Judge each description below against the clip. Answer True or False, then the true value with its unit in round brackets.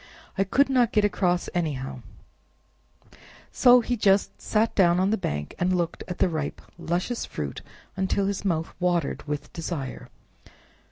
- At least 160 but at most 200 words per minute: False (150 wpm)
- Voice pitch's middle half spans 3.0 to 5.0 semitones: True (3.9 semitones)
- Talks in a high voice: False (180 Hz)